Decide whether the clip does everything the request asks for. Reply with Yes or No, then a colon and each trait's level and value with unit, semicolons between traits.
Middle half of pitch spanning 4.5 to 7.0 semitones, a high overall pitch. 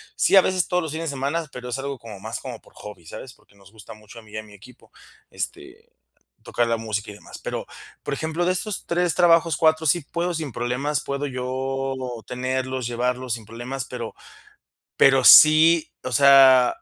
No: average, 5.1 semitones; low, 130 Hz